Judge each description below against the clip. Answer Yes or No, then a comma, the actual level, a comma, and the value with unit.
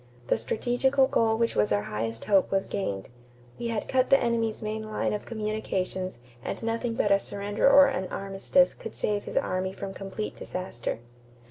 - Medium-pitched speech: No, high, 210 Hz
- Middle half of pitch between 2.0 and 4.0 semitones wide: Yes, average, 3.4 semitones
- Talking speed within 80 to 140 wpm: No, average, 175 wpm